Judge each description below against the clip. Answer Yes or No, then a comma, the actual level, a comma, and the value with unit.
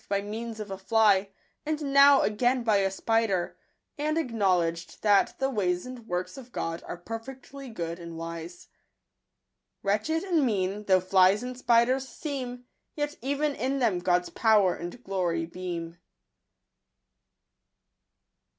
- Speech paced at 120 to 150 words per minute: Yes, average, 140 wpm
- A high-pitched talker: Yes, high, 210 Hz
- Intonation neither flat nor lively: No, wide, 5.8 semitones